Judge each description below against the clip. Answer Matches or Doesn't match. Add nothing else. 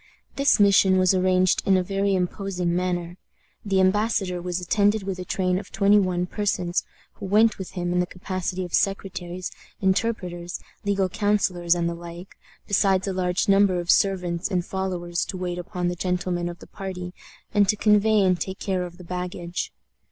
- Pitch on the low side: Doesn't match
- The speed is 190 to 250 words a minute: Doesn't match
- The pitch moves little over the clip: Matches